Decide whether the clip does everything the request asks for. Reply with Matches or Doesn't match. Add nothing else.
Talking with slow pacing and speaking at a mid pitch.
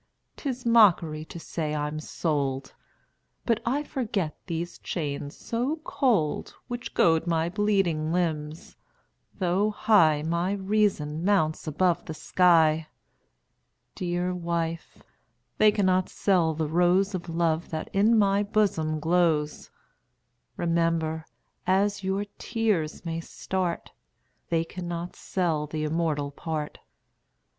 Matches